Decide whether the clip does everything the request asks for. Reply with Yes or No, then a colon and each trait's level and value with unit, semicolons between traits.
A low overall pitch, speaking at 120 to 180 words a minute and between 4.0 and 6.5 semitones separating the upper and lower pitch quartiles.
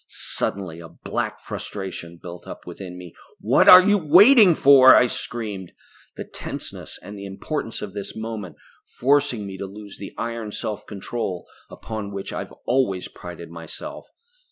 Yes: low, 105 Hz; average, 155 wpm; average, 4.9 semitones